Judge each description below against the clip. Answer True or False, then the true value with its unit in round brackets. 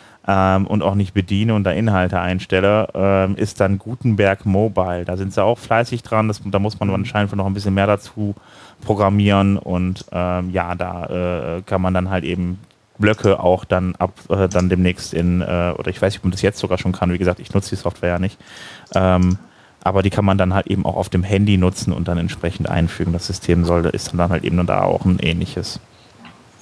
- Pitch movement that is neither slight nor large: False (1.9 semitones)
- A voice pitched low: True (95 Hz)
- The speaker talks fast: True (220 wpm)